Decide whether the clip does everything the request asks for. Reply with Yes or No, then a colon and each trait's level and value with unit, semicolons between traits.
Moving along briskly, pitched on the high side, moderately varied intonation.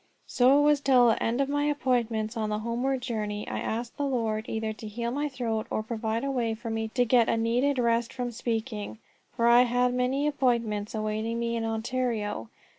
No: fast, 210 wpm; high, 235 Hz; narrow, 2.3 semitones